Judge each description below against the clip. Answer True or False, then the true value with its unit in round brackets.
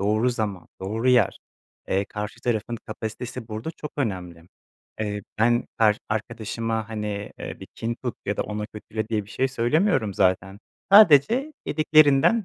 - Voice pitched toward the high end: False (110 Hz)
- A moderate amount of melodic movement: True (3.3 semitones)